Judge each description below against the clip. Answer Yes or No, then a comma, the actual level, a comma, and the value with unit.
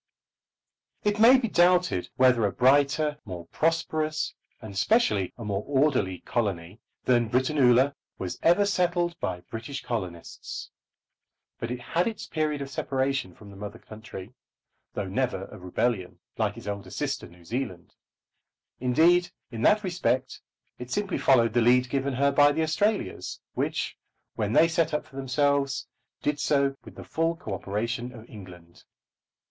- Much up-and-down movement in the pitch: Yes, wide, 6.4 semitones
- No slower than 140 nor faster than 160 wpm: Yes, average, 150 wpm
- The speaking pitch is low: Yes, low, 130 Hz